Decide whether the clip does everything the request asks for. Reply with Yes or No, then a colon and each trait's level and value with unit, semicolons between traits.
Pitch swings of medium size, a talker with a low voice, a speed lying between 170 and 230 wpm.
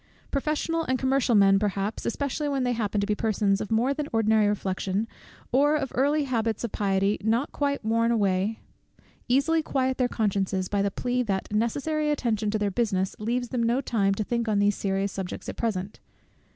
No: average, 4.3 semitones; high, 225 Hz; average, 190 wpm